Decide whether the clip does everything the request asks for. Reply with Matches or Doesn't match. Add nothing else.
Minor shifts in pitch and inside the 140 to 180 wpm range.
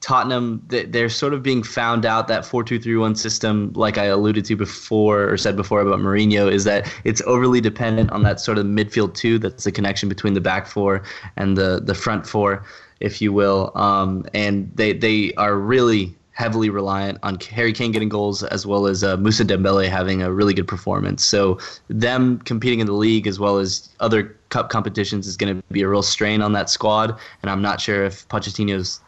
Doesn't match